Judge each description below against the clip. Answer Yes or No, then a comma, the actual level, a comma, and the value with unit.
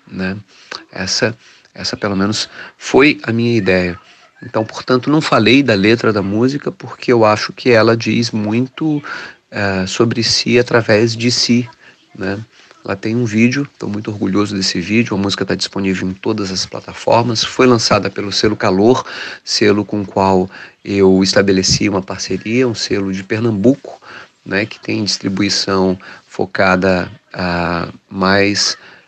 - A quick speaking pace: No, average, 145 wpm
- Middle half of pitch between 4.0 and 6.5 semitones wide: No, average, 3.4 semitones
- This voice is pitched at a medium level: No, low, 105 Hz